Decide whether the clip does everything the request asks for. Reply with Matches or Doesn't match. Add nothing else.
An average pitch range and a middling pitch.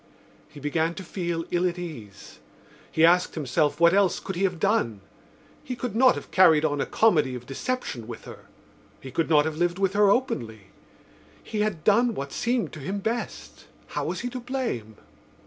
Doesn't match